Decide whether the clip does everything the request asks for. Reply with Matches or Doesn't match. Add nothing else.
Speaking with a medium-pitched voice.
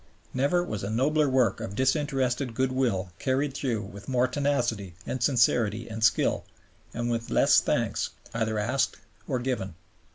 Doesn't match